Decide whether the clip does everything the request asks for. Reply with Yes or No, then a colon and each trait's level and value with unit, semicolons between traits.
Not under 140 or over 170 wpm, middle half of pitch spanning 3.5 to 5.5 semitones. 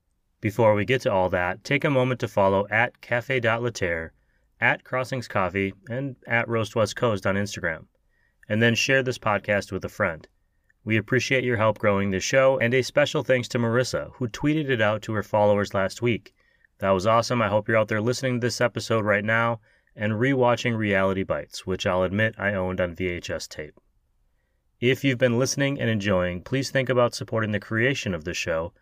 No: average, 200 wpm; average, 4.2 semitones